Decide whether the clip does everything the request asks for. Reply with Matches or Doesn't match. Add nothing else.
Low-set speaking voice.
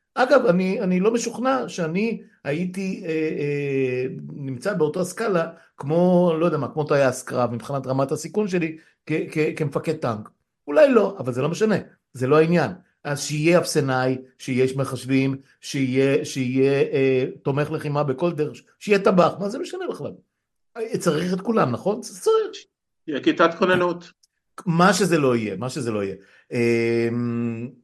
Doesn't match